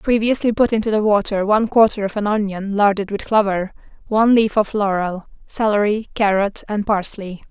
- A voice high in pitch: Yes, high, 205 Hz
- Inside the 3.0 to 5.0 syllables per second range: No, 5.3 syllables/s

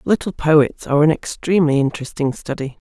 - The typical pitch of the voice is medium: Yes, medium, 150 Hz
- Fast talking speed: No, average, 145 wpm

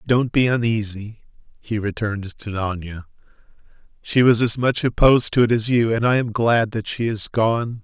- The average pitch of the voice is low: Yes, low, 110 Hz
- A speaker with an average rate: Yes, average, 185 wpm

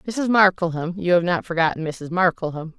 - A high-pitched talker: No, medium, 175 Hz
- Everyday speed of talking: Yes, average, 150 wpm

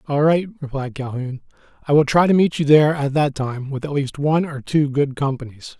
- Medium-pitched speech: Yes, medium, 145 Hz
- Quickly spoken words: Yes, fast, 230 wpm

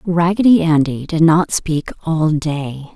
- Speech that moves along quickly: No, average, 140 wpm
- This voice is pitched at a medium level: Yes, medium, 160 Hz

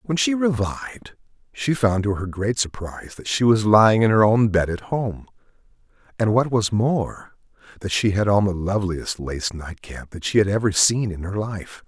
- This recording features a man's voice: Yes, male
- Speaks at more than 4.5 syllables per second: Yes, 4.8 syllables/s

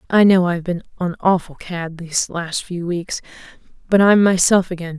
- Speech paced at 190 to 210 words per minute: No, average, 180 wpm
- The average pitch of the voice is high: No, medium, 180 Hz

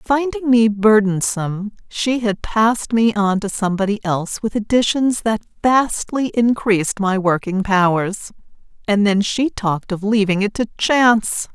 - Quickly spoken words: No, average, 145 wpm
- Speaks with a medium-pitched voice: No, high, 215 Hz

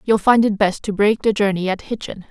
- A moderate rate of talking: No, fast, 260 wpm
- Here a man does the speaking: No, female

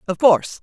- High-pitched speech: No, medium, 170 Hz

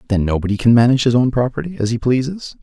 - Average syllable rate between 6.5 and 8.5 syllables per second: Yes, 7.2 syllables/s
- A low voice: Yes, low, 120 Hz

